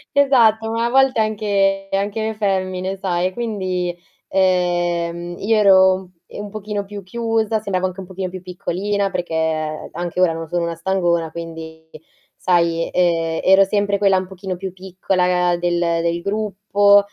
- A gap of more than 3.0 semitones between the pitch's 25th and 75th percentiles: No, average, 2.7 semitones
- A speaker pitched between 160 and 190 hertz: Yes, medium, 185 Hz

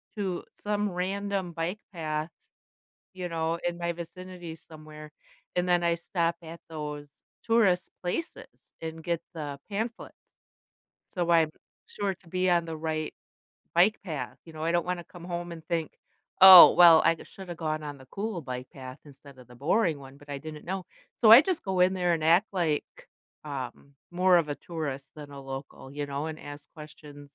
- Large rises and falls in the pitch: No, average, 3.2 semitones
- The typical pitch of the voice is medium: Yes, medium, 165 Hz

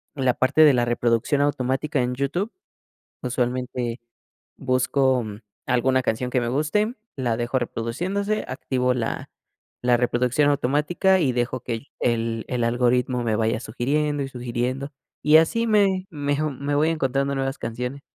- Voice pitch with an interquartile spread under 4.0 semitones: Yes, average, 3.1 semitones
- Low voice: Yes, low, 130 Hz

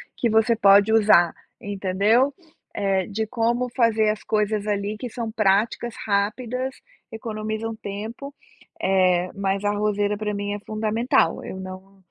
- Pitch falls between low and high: No, high, 210 Hz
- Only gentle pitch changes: Yes, narrow, 2.1 semitones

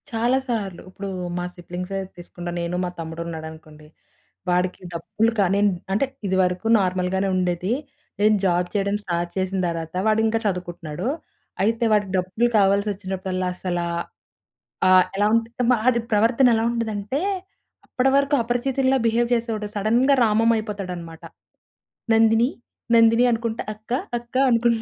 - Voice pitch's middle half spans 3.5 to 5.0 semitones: Yes, average, 4.1 semitones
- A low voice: No, high, 205 Hz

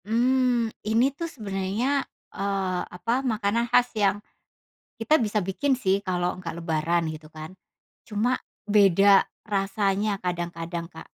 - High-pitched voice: Yes, high, 200 Hz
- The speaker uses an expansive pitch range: No, average, 4.0 semitones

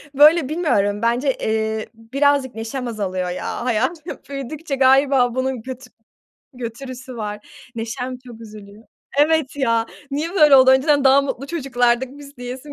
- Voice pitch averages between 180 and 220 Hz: No, very high, 255 Hz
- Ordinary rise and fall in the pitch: Yes, average, 3.5 semitones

